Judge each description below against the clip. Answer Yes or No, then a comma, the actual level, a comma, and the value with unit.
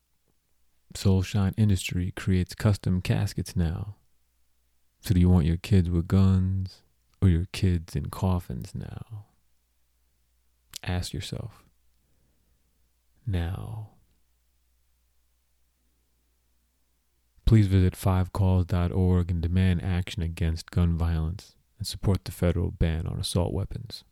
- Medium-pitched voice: No, very low, 85 Hz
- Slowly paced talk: Yes, slow, 100 wpm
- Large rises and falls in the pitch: Yes, wide, 7.6 semitones